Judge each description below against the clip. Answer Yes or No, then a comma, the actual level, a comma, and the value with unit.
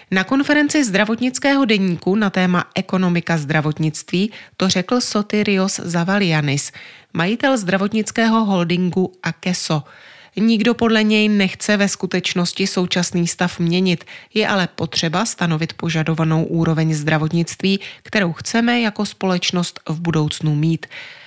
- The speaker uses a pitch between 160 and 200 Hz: Yes, medium, 185 Hz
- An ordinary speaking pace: No, slow, 110 wpm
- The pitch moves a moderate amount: Yes, average, 4.0 semitones